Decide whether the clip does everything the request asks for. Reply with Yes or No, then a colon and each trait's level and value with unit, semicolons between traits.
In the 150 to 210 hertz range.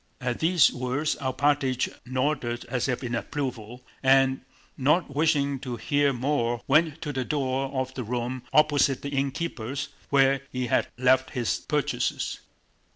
No: low, 135 Hz